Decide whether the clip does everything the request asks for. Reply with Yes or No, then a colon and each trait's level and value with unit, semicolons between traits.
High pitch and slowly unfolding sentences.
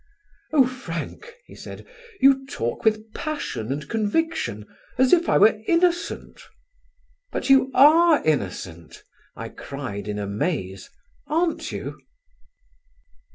Yes: high, 220 Hz; slow, 110 wpm